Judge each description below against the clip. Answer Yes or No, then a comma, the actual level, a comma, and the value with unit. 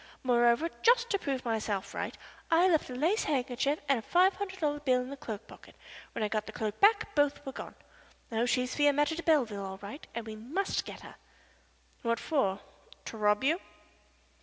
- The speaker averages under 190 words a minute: No, average, 195 wpm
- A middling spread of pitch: No, wide, 6.3 semitones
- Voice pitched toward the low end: No, very high, 265 Hz